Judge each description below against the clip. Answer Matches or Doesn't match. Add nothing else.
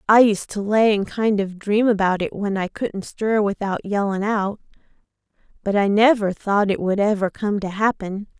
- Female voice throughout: Matches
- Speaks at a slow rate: Doesn't match